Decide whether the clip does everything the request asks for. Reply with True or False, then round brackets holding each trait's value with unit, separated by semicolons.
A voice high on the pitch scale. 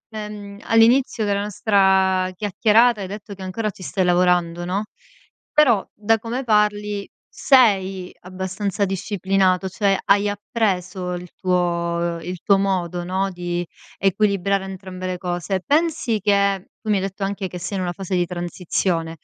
True (195 Hz)